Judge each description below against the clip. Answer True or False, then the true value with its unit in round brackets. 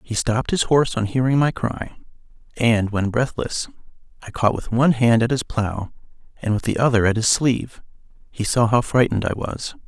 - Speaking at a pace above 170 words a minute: True (195 wpm)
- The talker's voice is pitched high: False (115 Hz)